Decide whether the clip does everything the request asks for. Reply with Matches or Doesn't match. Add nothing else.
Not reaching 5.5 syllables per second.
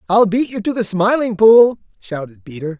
Matches